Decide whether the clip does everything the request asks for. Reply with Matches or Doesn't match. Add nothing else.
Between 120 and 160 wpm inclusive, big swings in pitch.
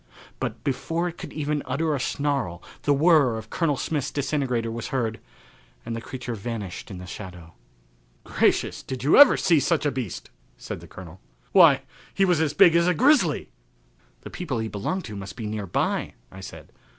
Doesn't match